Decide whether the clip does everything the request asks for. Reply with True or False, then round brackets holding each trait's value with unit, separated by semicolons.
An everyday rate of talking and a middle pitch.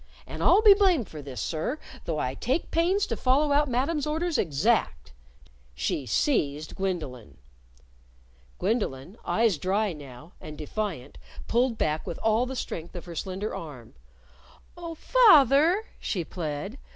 False (145 wpm; 205 Hz)